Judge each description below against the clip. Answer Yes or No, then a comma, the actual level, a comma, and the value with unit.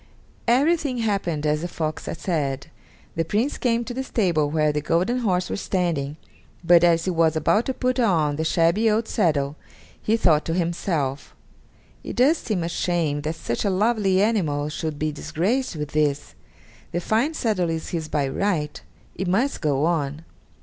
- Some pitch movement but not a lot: No, wide, 5.8 semitones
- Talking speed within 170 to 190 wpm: Yes, average, 175 wpm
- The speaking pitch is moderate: Yes, medium, 170 Hz